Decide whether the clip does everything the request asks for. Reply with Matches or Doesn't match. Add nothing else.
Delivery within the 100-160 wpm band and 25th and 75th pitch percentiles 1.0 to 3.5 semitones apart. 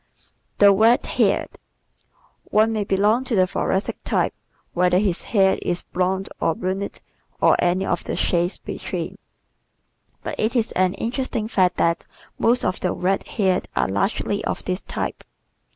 Matches